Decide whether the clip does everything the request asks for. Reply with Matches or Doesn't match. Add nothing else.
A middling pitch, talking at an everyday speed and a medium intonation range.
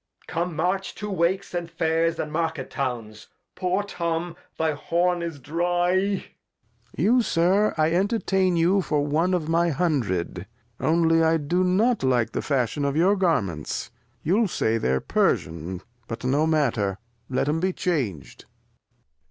Matches